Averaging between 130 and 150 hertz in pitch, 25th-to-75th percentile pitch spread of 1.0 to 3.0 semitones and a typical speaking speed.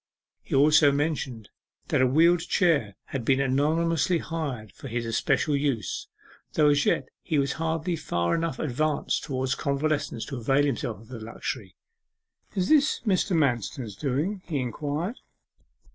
No: medium, 140 Hz; average, 4.3 semitones; average, 145 wpm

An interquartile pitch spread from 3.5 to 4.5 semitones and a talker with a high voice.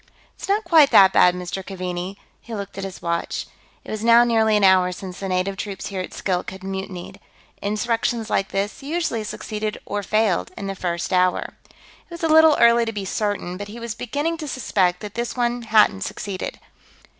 Yes: average, 3.8 semitones; high, 205 Hz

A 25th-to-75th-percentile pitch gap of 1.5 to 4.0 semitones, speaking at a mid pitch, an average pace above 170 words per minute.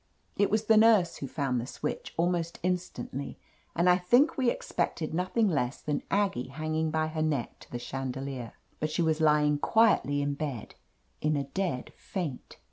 No: average, 4.5 semitones; medium, 155 Hz; average, 180 wpm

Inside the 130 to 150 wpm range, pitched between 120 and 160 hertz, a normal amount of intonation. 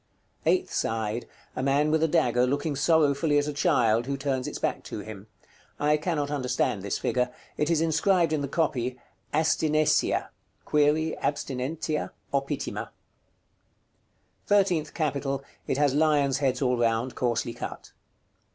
Yes: average, 140 wpm; medium, 140 Hz; average, 3.4 semitones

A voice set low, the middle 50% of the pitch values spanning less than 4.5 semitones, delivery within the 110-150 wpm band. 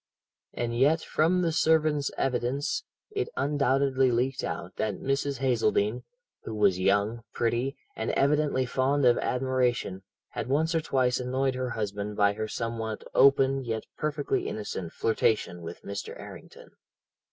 Yes: low, 125 Hz; average, 4.1 semitones; average, 140 wpm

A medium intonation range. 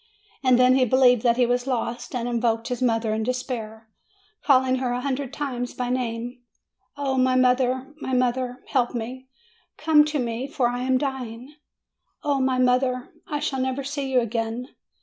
No: narrow, 1.4 semitones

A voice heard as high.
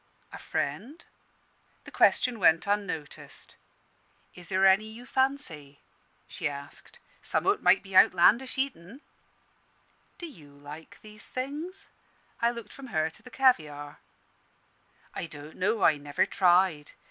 Yes: high, 195 Hz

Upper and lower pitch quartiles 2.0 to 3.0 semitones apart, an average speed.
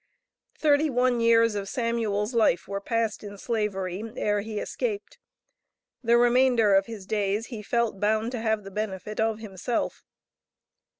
Yes: narrow, 2.5 semitones; average, 145 wpm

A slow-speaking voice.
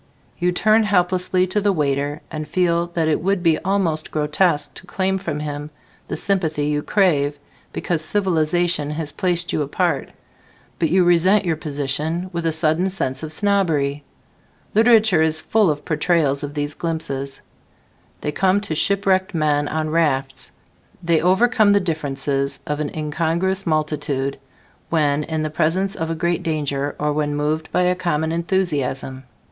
No: average, 155 wpm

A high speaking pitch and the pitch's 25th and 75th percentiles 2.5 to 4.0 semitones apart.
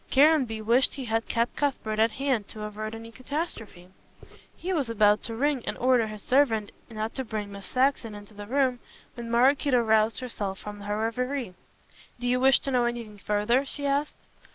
Yes: high, 230 Hz; average, 3.5 semitones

